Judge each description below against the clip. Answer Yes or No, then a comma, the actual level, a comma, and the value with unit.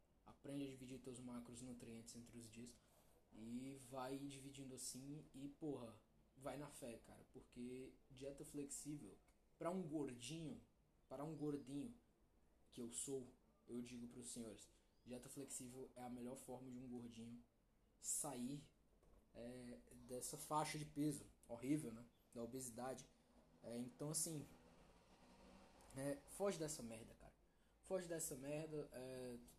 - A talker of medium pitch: No, low, 125 Hz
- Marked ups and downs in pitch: No, average, 3.2 semitones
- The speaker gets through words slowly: No, average, 140 wpm